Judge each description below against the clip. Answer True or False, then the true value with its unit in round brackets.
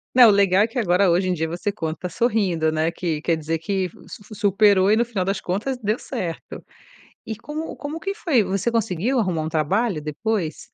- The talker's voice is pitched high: True (195 Hz)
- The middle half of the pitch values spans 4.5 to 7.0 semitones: True (5.0 semitones)